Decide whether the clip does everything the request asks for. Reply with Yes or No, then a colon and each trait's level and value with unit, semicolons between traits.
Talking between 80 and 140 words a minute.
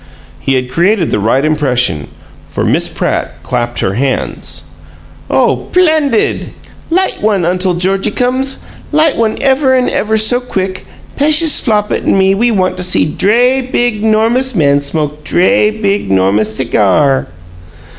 Yes: slow, 135 wpm